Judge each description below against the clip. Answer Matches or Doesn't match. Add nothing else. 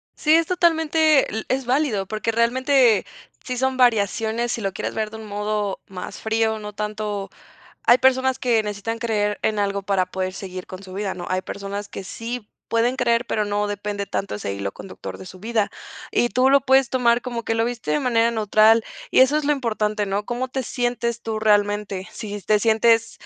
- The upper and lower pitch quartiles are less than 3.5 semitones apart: Matches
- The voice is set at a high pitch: Matches